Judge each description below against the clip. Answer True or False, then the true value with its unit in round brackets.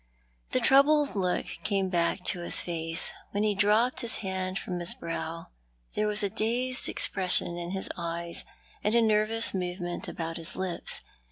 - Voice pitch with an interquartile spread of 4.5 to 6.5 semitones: False (3.7 semitones)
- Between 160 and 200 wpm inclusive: True (165 wpm)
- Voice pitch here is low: False (190 Hz)